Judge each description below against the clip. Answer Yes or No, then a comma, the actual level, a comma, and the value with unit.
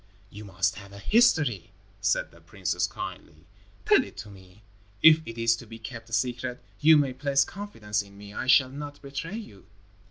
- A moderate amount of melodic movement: No, wide, 5.9 semitones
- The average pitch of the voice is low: Yes, low, 115 Hz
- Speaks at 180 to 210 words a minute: Yes, average, 190 wpm